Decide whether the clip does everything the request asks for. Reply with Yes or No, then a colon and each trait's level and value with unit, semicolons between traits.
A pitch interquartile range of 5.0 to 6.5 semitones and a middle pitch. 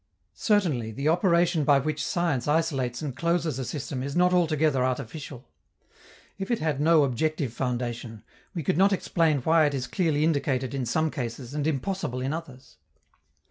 No: average, 4.3 semitones; medium, 145 Hz